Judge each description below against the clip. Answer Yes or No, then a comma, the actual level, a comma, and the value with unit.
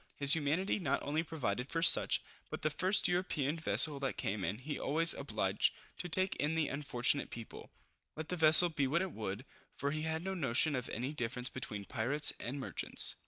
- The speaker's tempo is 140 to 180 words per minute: No, average, 195 wpm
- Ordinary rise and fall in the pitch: Yes, average, 4.4 semitones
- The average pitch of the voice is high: No, medium, 145 Hz